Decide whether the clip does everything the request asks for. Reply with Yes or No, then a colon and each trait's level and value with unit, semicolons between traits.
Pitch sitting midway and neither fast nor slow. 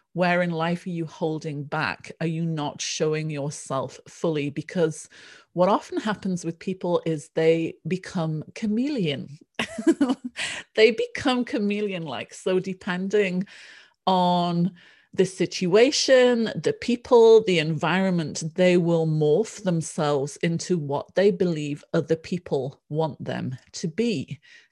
No: medium, 175 Hz; slow, 120 wpm